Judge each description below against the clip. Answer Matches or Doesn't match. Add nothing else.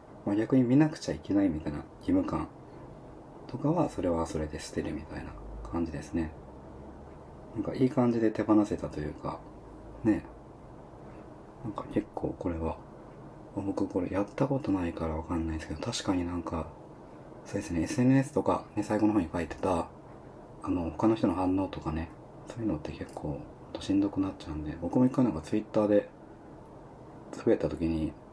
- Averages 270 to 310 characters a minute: Doesn't match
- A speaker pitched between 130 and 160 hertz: Doesn't match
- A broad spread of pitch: Matches